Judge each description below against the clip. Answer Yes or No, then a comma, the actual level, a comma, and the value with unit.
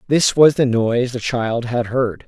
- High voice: No, low, 125 Hz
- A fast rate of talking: Yes, fast, 210 wpm